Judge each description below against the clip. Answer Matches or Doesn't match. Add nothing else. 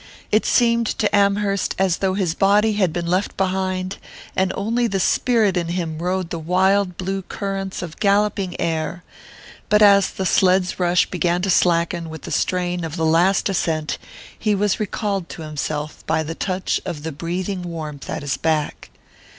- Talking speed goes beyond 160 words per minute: Matches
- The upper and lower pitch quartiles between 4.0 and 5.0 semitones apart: Doesn't match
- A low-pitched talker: Doesn't match